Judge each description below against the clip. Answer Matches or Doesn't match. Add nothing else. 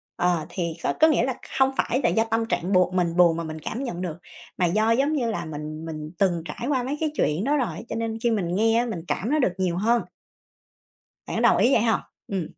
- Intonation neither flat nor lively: Doesn't match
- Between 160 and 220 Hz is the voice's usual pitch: Matches